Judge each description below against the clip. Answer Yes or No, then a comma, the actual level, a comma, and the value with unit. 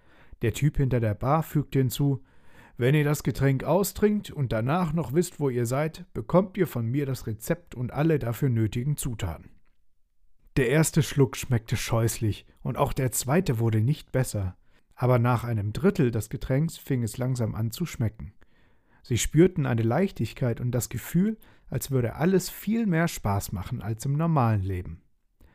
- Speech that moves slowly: No, average, 170 wpm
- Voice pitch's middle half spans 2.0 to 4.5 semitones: No, average, 4.9 semitones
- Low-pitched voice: Yes, low, 130 Hz